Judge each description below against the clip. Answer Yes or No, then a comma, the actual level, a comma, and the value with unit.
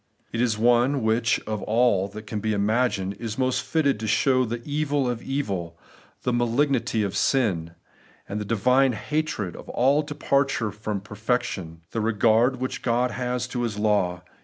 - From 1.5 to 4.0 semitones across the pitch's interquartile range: Yes, average, 3.3 semitones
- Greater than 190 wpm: No, average, 160 wpm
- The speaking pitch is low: Yes, low, 115 Hz